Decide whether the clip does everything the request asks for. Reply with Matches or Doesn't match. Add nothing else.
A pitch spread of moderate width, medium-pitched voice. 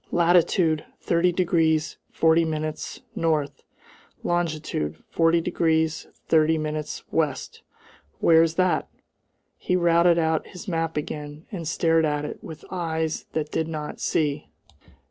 Doesn't match